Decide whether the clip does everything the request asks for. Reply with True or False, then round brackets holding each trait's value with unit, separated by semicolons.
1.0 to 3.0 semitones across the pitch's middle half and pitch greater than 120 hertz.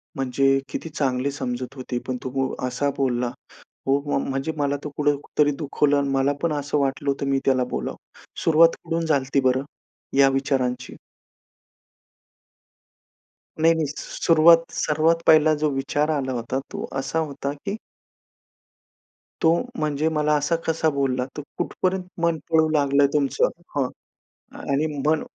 True (2.5 semitones; 140 Hz)